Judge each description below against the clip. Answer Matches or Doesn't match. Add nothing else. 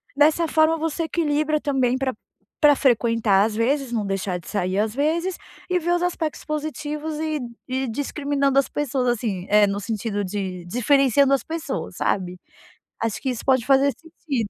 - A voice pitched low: Doesn't match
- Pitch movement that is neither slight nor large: Doesn't match